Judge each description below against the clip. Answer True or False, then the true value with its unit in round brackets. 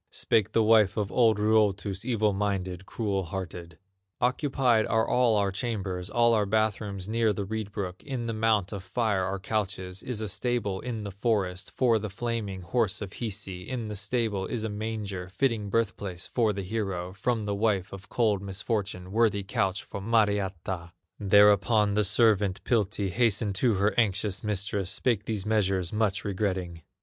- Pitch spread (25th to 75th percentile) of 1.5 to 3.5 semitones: True (2.5 semitones)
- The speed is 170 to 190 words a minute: True (175 wpm)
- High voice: False (105 Hz)